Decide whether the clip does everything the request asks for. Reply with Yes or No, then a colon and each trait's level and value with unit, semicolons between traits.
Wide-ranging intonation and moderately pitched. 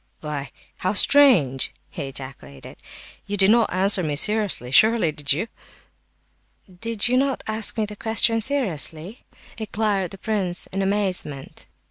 No: wide, 6.3 semitones; high, 195 Hz